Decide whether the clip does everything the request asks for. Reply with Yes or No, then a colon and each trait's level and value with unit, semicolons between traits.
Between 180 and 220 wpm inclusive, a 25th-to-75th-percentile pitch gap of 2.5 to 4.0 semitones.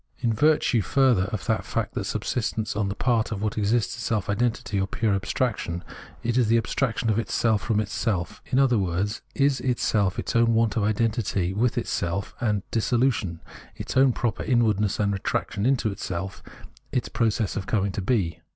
Yes: average, 190 wpm; average, 3.1 semitones